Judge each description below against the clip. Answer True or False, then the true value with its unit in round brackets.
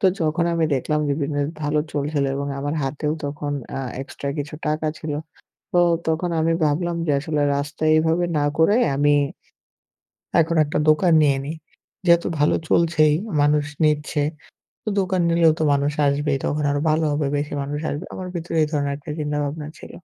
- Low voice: False (150 Hz)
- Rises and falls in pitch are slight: True (1.9 semitones)